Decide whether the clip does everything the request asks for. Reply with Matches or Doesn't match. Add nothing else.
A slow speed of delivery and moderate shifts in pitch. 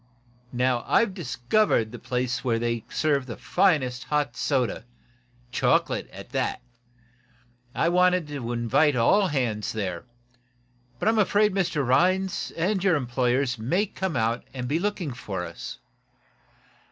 Doesn't match